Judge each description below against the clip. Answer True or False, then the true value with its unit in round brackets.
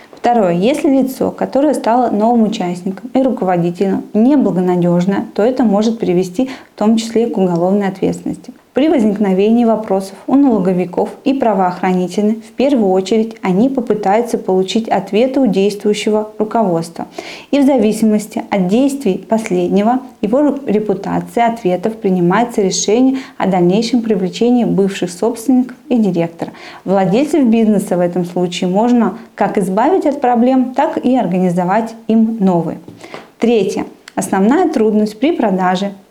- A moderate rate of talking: True (125 wpm)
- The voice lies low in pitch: False (215 Hz)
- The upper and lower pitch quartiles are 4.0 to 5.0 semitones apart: True (4.3 semitones)